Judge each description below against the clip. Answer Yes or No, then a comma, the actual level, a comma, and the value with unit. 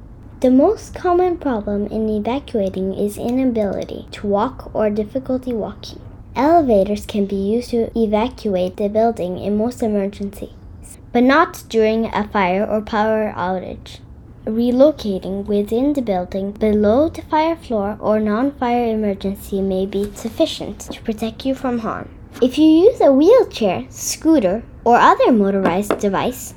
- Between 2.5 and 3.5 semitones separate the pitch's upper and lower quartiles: No, average, 4.1 semitones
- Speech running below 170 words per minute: Yes, average, 140 wpm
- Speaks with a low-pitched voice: No, high, 220 Hz